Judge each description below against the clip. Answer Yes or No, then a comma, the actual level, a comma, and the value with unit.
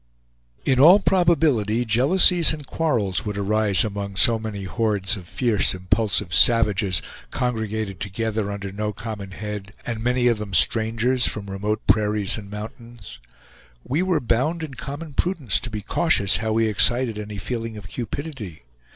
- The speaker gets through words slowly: No, average, 150 wpm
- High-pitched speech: No, low, 110 Hz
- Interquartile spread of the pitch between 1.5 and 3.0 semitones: No, average, 3.5 semitones